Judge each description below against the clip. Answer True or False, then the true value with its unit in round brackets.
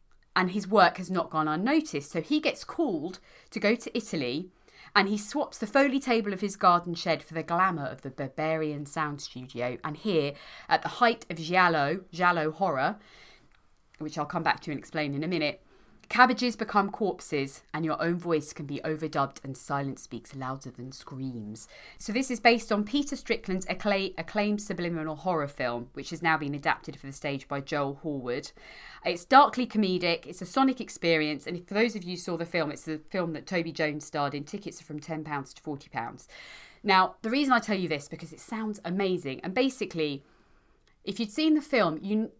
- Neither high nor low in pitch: True (170 Hz)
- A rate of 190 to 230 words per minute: True (200 wpm)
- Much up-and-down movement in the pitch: True (5.8 semitones)